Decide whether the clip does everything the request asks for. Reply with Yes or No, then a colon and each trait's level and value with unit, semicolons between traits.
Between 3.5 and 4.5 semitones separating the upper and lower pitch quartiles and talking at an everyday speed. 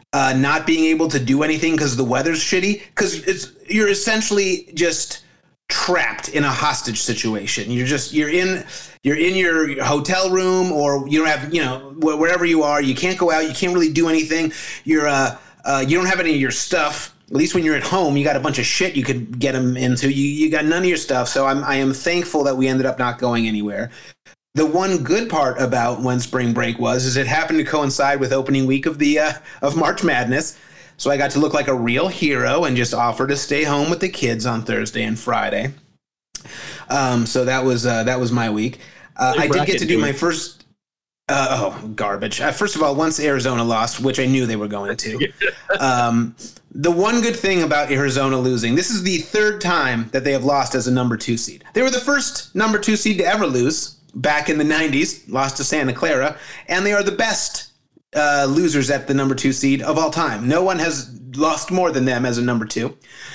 No: average, 4.2 semitones; fast, 225 wpm